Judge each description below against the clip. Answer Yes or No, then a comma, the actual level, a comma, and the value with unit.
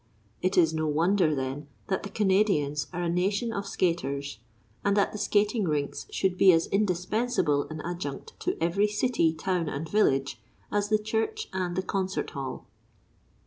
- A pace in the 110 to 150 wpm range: No, average, 165 wpm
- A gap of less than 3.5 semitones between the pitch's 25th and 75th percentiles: No, average, 4.7 semitones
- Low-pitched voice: No, medium, 180 Hz